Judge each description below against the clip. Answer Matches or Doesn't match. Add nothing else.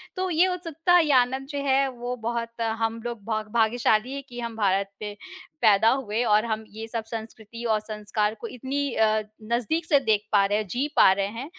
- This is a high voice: Matches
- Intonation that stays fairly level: Doesn't match